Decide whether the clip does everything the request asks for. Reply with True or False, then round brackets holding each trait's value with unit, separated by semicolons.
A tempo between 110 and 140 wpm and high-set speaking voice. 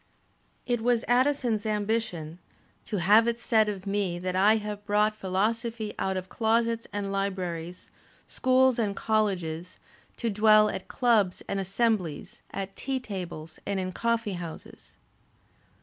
True (135 wpm; 210 Hz)